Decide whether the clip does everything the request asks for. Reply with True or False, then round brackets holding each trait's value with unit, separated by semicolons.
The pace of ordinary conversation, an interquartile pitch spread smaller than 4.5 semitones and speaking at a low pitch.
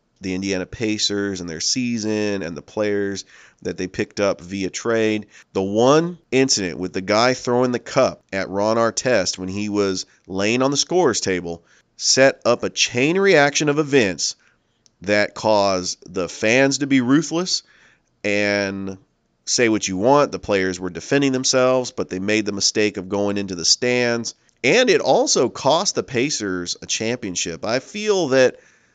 False (165 wpm; 5.0 semitones; 105 Hz)